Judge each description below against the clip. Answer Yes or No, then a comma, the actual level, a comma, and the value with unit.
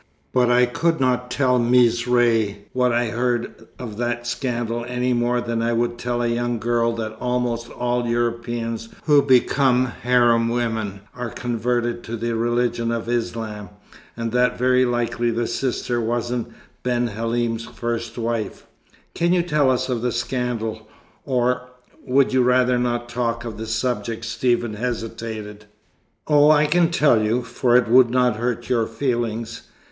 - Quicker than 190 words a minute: No, average, 160 wpm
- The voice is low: Yes, low, 120 Hz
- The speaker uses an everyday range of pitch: No, narrow, 1.2 semitones